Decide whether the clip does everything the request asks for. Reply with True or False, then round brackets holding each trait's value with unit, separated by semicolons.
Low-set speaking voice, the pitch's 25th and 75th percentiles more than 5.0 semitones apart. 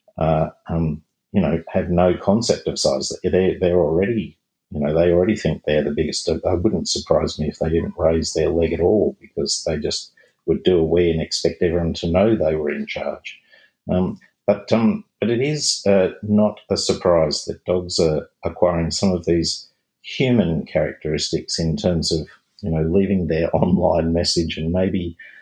False (85 Hz; 3.2 semitones)